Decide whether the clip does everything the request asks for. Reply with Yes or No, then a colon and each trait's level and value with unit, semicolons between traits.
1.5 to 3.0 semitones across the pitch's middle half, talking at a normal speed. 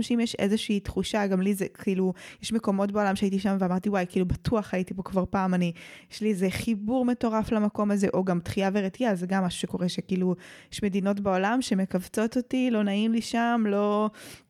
No: narrow, 2.6 semitones; fast, 200 wpm